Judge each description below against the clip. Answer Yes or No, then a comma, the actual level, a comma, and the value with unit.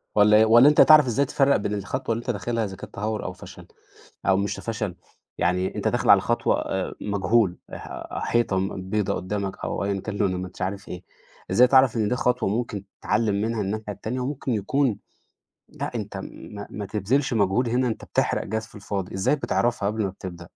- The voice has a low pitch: Yes, low, 105 Hz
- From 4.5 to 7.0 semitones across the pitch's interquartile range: No, average, 3.4 semitones